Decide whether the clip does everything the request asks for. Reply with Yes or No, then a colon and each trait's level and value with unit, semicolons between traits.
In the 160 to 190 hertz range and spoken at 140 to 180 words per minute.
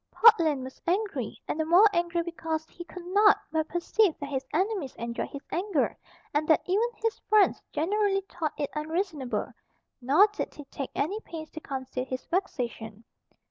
No: very high, 325 Hz; average, 170 wpm